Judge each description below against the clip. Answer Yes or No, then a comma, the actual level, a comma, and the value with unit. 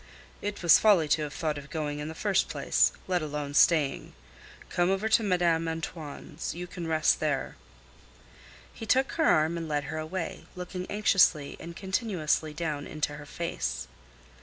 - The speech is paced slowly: No, average, 165 wpm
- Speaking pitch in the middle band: Yes, medium, 165 Hz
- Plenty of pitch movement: No, average, 3.2 semitones